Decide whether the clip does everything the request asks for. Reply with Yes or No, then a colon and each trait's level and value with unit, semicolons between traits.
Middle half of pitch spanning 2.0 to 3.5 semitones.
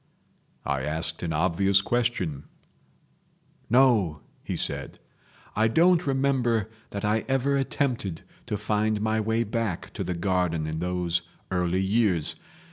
No: average, 5.2 semitones